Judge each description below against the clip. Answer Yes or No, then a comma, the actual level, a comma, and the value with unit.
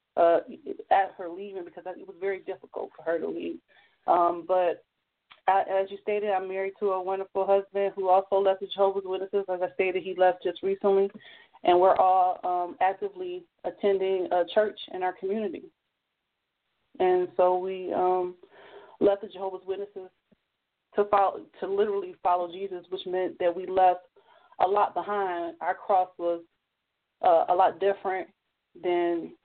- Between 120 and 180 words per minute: Yes, average, 160 wpm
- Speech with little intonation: Yes, narrow, 1.6 semitones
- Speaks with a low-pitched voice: No, high, 190 Hz